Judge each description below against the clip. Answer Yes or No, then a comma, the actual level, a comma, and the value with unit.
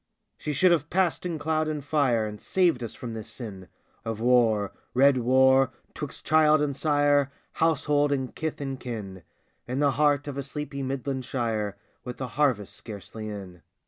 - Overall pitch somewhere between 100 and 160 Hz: Yes, low, 135 Hz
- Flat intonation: No, average, 4.3 semitones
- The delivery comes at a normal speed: Yes, average, 180 wpm